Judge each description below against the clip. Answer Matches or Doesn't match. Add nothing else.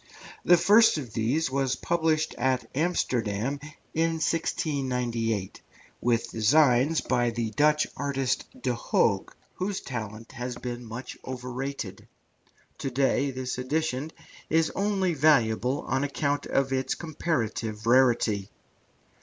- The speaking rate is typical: Doesn't match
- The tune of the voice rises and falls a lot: Doesn't match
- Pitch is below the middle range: Matches